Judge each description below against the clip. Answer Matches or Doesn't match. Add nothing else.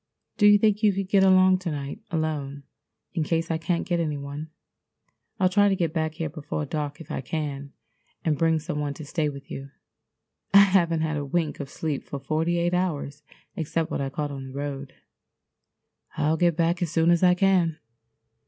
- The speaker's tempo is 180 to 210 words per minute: Matches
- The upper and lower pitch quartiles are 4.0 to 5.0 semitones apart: Doesn't match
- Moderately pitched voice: Matches